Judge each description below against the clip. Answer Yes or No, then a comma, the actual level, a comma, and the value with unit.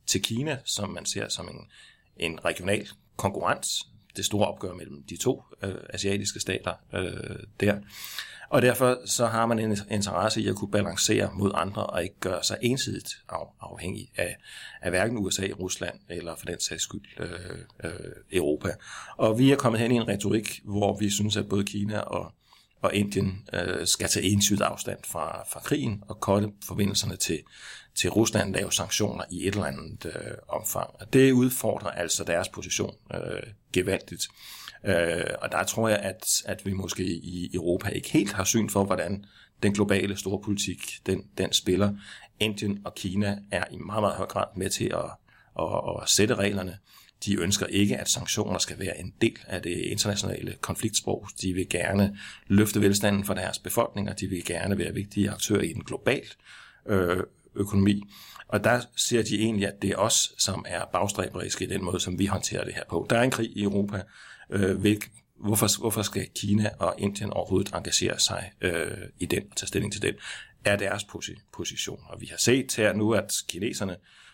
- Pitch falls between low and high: No, low, 100 Hz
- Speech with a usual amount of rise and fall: No, narrow, 1.7 semitones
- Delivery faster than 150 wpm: Yes, average, 180 wpm